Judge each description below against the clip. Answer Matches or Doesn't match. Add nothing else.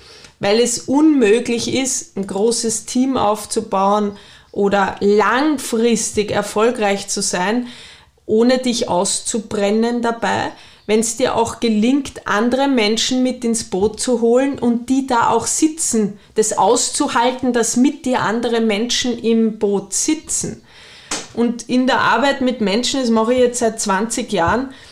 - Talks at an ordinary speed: Matches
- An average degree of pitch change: Matches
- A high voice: Matches